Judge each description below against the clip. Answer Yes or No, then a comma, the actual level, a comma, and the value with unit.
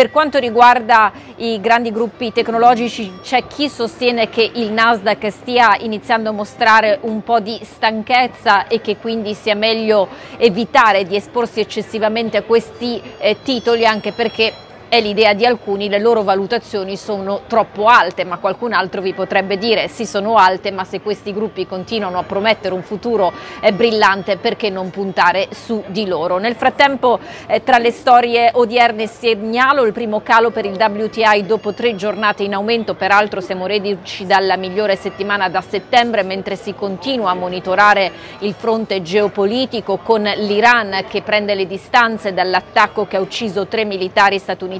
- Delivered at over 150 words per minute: Yes, average, 160 wpm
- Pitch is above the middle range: Yes, high, 215 Hz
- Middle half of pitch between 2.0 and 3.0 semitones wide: Yes, average, 2.7 semitones